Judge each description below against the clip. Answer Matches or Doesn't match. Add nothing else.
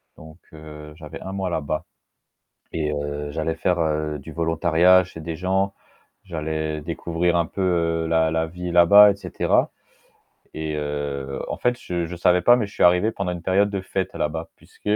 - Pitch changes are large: Doesn't match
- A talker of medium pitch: Doesn't match